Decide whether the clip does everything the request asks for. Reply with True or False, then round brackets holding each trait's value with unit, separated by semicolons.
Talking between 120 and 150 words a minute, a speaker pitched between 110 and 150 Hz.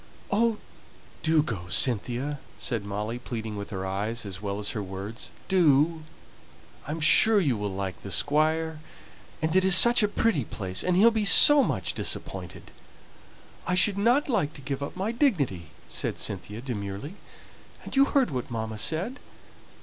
False (165 wpm; 140 Hz)